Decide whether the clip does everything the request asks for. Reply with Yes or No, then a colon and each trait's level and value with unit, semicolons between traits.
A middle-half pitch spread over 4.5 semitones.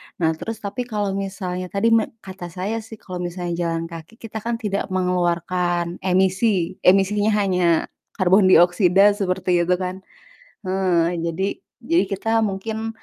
No: average, 2.7 semitones